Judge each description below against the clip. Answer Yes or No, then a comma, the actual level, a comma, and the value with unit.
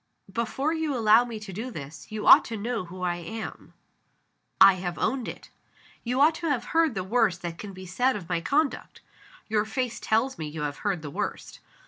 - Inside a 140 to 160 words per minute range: No, fast, 205 wpm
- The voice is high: Yes, high, 215 Hz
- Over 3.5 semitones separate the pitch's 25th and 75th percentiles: Yes, wide, 5.6 semitones